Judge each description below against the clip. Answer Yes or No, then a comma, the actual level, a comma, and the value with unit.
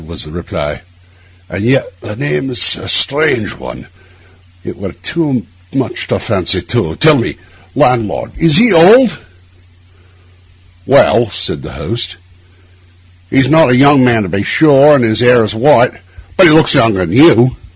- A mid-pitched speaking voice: No, low, 125 Hz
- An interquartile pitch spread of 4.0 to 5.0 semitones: No, wide, 5.5 semitones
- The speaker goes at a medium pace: Yes, average, 160 wpm